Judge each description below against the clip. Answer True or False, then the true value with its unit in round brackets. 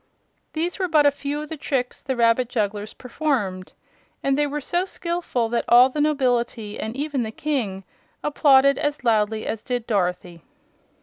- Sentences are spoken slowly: False (170 wpm)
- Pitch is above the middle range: True (255 Hz)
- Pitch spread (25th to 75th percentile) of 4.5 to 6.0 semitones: True (4.9 semitones)